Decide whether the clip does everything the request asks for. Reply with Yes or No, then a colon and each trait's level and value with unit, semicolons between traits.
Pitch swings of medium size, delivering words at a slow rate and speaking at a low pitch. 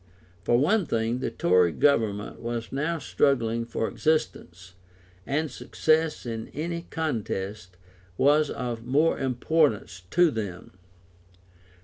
No: wide, 6.0 semitones; slow, 110 wpm; low, 120 Hz